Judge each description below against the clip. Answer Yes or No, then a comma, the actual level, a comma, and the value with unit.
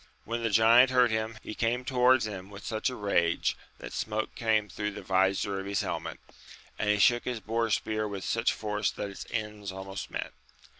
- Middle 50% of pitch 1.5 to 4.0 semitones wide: Yes, narrow, 2.4 semitones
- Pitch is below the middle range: Yes, low, 110 Hz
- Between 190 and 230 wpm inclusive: Yes, average, 195 wpm